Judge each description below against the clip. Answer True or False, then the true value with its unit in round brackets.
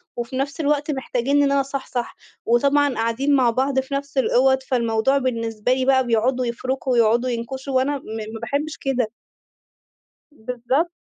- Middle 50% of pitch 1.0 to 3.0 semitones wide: True (2.6 semitones)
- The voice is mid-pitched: False (260 Hz)